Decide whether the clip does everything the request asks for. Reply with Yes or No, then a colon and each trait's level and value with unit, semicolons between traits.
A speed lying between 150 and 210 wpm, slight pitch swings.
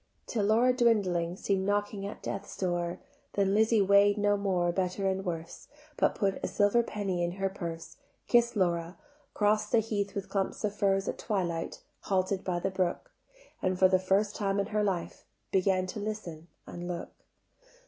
Yes: average, 175 wpm; narrow, 2.2 semitones